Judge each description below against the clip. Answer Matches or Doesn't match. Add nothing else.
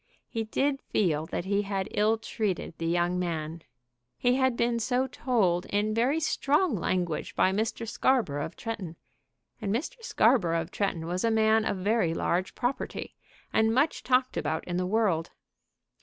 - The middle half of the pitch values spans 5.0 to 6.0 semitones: Matches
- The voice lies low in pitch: Doesn't match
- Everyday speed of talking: Matches